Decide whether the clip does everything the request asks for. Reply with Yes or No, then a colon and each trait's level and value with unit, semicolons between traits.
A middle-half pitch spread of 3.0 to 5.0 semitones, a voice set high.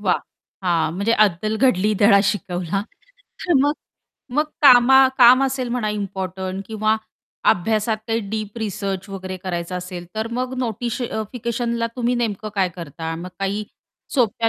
Yes: average, 4.0 semitones; high, 215 Hz